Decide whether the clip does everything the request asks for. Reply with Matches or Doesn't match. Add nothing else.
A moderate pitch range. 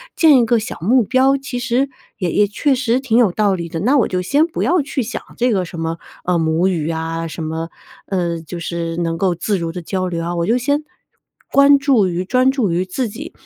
Doesn't match